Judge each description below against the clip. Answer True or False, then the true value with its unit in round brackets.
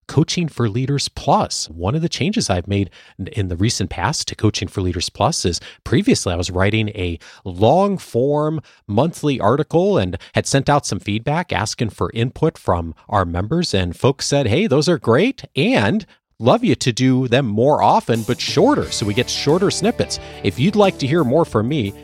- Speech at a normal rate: True (195 wpm)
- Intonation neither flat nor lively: False (6.9 semitones)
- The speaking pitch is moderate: False (115 Hz)